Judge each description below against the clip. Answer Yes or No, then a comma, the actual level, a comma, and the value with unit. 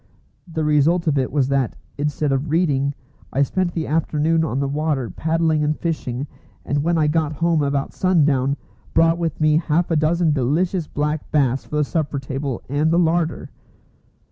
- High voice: No, medium, 150 Hz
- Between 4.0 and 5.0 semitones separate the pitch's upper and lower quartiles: No, average, 2.7 semitones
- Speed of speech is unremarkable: Yes, average, 175 wpm